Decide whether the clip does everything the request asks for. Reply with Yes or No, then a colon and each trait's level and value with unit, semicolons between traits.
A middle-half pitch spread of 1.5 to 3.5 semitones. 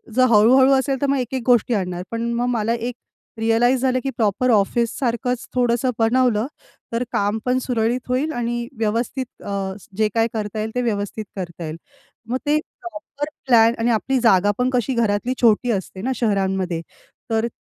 Yes: average, 3.0 semitones